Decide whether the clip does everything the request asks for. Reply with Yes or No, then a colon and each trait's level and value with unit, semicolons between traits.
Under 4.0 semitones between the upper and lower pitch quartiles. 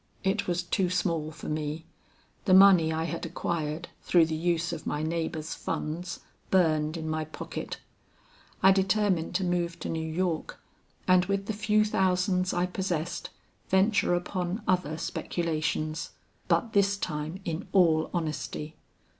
Yes: average, 2.9 semitones